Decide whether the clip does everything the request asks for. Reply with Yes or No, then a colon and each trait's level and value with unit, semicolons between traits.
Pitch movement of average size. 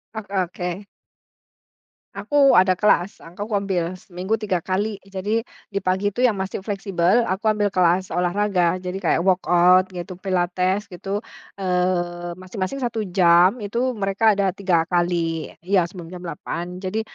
No: narrow, 2.2 semitones